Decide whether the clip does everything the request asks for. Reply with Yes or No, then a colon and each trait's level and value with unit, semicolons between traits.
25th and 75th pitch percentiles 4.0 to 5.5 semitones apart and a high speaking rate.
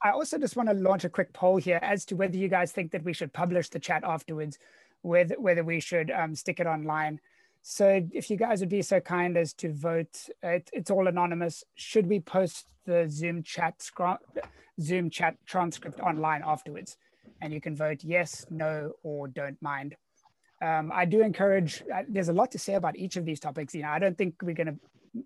No: average, 3.2 semitones; fast, 215 wpm